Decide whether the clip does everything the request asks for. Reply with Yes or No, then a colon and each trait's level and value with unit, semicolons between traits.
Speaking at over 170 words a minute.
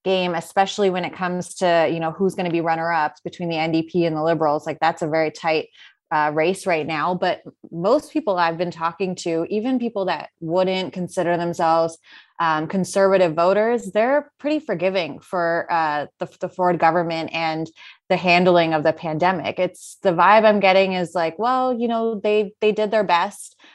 Yes: average, 185 wpm